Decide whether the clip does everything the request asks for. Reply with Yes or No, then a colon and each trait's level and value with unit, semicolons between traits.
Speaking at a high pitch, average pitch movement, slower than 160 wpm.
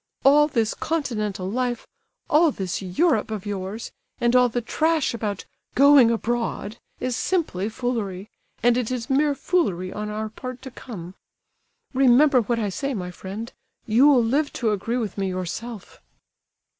Yes: high, 235 Hz; average, 4.3 semitones; average, 150 wpm